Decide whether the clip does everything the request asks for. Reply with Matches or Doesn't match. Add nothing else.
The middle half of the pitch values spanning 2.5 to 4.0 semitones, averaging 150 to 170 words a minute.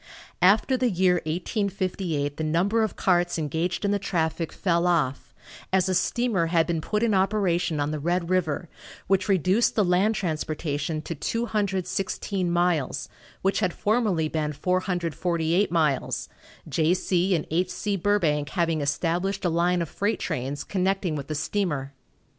Matches